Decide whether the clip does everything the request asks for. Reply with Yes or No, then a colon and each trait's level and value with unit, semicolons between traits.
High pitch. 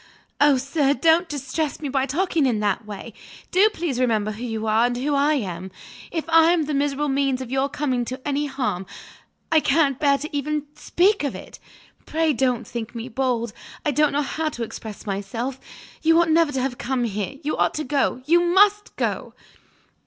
Yes: very high, 275 Hz